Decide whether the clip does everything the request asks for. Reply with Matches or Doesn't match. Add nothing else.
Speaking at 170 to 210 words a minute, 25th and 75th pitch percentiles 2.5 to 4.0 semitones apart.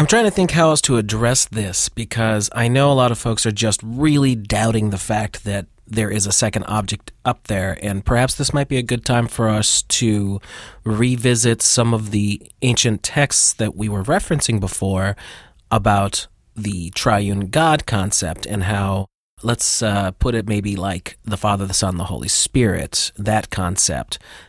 Matches